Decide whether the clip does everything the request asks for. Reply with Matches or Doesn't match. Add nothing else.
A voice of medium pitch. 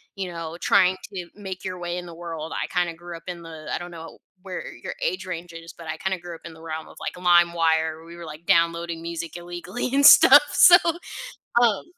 Matches